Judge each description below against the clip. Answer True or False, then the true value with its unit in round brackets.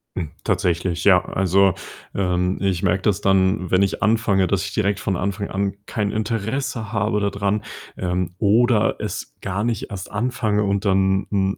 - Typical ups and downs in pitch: False (1.9 semitones)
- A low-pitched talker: True (100 Hz)